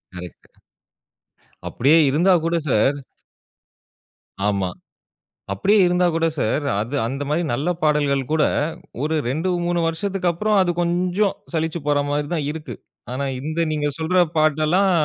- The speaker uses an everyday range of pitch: Yes, average, 3.5 semitones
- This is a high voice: No, medium, 155 Hz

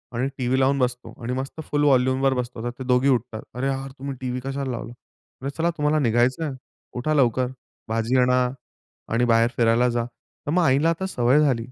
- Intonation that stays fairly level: Yes, narrow, 2.2 semitones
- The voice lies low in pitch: Yes, low, 130 Hz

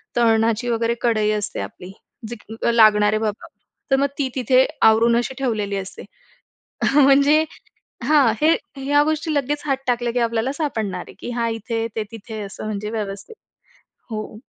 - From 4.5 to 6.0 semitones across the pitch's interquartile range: No, average, 3.9 semitones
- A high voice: Yes, high, 230 Hz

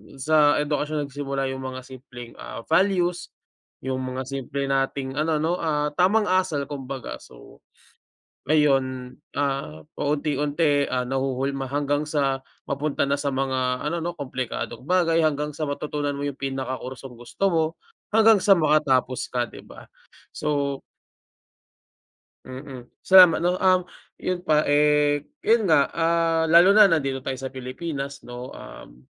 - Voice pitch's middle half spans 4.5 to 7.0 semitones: No, average, 3.1 semitones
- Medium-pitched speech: Yes, medium, 145 Hz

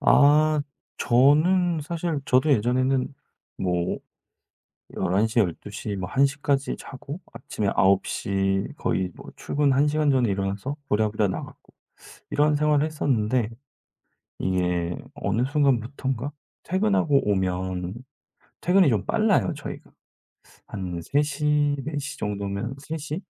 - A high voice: No, low, 130 Hz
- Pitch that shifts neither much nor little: No, wide, 7.0 semitones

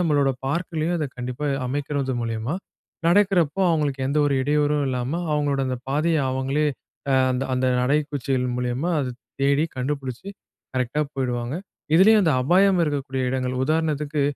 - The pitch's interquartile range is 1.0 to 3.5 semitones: Yes, average, 3.0 semitones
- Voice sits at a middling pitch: Yes, medium, 145 Hz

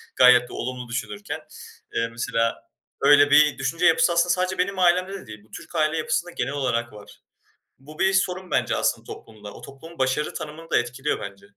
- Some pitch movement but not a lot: No, wide, 6.3 semitones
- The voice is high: No, medium, 140 Hz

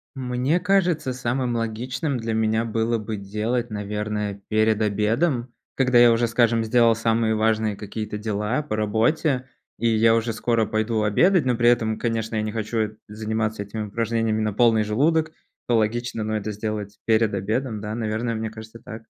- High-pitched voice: No, low, 110 Hz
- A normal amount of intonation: No, narrow, 1.9 semitones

